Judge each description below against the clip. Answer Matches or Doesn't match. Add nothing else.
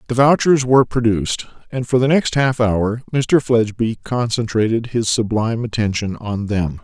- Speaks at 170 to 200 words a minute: Doesn't match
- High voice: Doesn't match